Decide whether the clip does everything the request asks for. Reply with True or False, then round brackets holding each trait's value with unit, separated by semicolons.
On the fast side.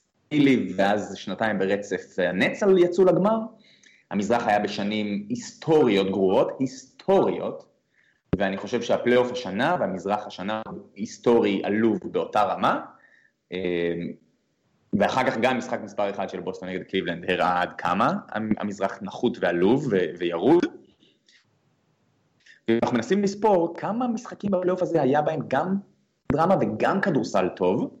False (115 wpm)